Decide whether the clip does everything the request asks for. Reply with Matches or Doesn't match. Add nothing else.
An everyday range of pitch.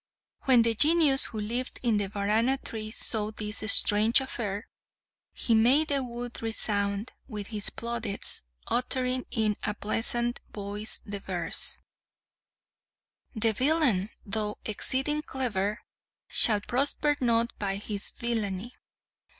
Matches